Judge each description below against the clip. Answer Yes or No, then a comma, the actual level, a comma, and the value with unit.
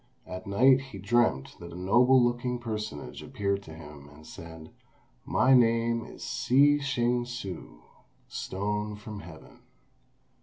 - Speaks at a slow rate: Yes, slow, 130 wpm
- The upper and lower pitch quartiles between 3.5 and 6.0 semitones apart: Yes, average, 5.1 semitones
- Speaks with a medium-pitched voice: No, low, 105 Hz